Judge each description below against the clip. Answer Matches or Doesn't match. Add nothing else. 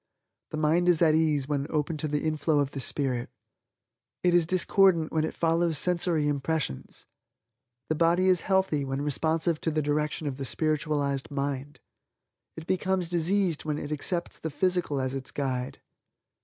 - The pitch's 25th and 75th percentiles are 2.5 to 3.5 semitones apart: Matches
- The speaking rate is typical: Matches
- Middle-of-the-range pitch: Matches